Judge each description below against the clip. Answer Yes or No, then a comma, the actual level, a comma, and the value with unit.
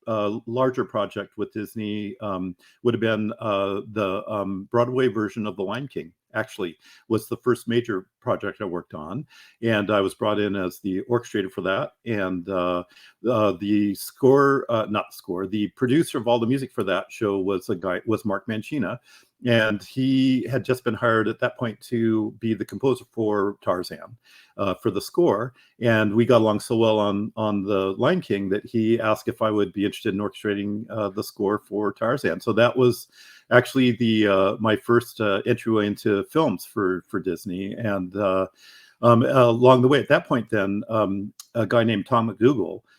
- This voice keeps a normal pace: Yes, average, 190 wpm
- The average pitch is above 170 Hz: No, low, 110 Hz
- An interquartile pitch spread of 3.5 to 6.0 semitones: No, average, 2.9 semitones